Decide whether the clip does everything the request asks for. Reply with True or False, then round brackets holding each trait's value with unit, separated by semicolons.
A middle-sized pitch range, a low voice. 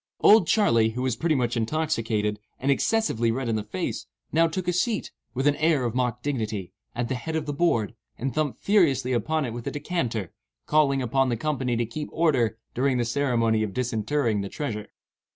True (5.0 semitones; 125 Hz)